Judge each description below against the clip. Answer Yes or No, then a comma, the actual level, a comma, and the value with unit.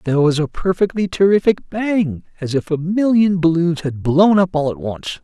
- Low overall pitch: No, medium, 170 Hz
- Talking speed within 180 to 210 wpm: Yes, average, 195 wpm